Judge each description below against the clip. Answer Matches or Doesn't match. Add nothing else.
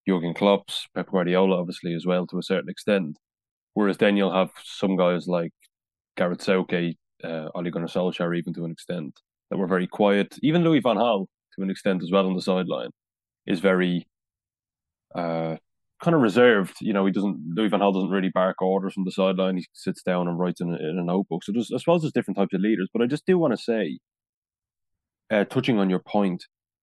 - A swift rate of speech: Matches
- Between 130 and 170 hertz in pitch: Doesn't match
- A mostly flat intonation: Matches